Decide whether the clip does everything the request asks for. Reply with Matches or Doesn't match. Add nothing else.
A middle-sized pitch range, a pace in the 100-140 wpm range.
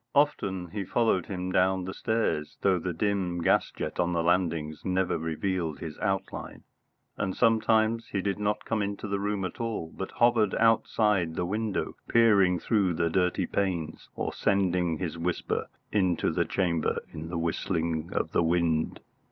Doesn't match